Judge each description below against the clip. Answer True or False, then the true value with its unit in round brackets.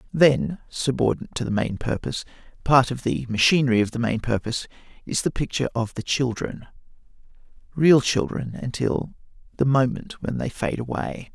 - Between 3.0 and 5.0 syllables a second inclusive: False (5.5 syllables/s)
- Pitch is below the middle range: True (125 Hz)